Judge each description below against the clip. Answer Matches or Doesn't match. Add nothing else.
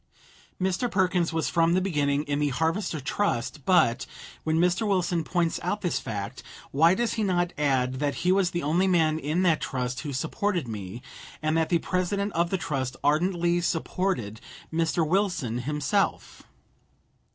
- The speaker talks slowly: Doesn't match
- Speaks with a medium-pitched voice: Matches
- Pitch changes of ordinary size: Matches